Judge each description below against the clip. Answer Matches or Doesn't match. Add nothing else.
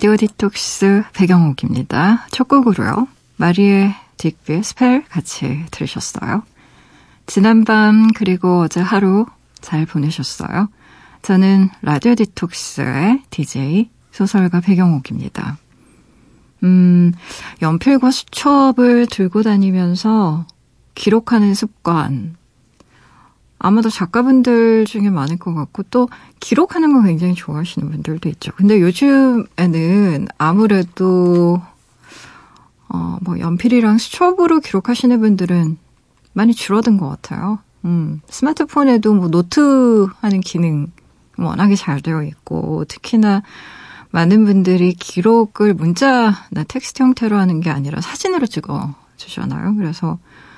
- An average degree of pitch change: Matches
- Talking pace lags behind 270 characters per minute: Matches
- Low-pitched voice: Doesn't match